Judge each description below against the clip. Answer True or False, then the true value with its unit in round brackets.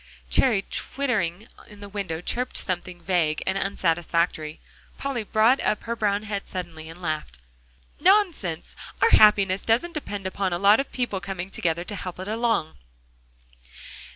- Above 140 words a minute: True (150 wpm)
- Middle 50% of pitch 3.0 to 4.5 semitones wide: True (4.2 semitones)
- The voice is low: False (195 Hz)